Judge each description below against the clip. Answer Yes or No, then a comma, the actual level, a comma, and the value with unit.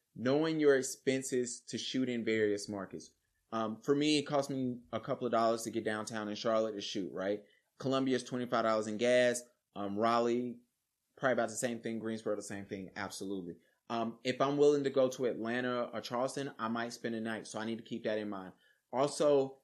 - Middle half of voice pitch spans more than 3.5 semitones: No, average, 2.9 semitones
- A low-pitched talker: Yes, low, 115 Hz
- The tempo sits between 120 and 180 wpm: No, fast, 205 wpm